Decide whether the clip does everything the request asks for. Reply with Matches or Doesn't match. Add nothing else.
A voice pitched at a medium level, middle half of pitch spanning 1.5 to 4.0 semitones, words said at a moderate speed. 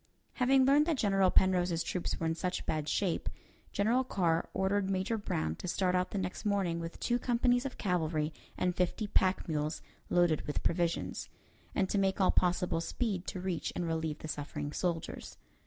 Matches